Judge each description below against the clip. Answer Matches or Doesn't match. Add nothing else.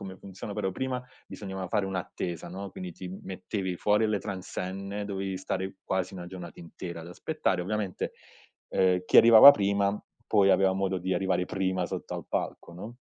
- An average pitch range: Doesn't match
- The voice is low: Matches